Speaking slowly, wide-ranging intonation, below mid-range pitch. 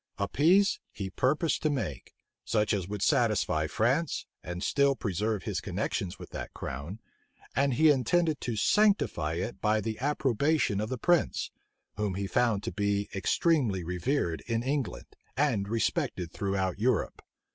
No: average, 150 wpm; wide, 6.4 semitones; low, 110 Hz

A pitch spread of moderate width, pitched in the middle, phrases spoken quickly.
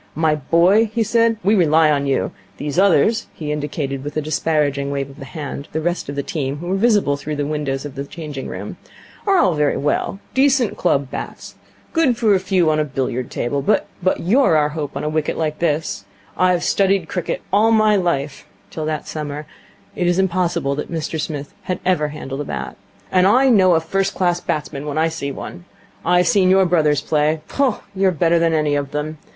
Yes: average, 4.2 semitones; medium, 160 Hz; fast, 210 wpm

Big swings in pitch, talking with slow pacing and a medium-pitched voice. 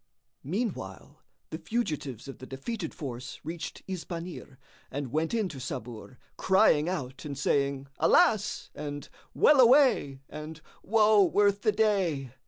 Yes: wide, 7.1 semitones; slow, 130 wpm; medium, 160 Hz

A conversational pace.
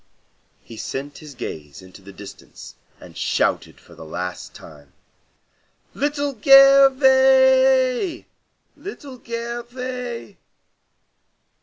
No: slow, 90 wpm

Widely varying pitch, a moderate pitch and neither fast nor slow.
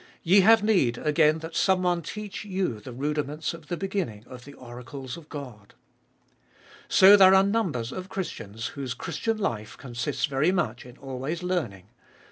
Yes: wide, 6.8 semitones; medium, 150 Hz; average, 165 wpm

